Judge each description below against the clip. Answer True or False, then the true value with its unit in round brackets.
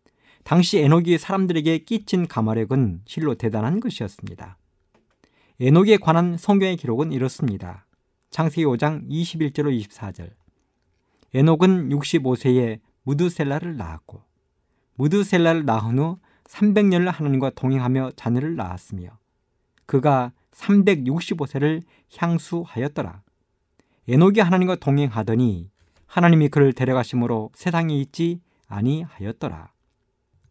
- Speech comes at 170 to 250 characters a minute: False (260 characters per minute)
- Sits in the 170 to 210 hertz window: False (140 Hz)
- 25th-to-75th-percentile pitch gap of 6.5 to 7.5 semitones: True (7.0 semitones)